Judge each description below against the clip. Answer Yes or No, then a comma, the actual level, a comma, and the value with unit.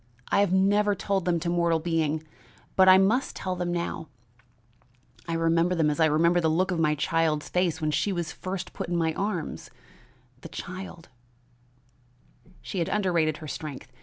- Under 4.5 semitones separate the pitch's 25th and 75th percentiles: Yes, average, 2.8 semitones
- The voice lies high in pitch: No, medium, 170 Hz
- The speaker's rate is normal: Yes, average, 180 wpm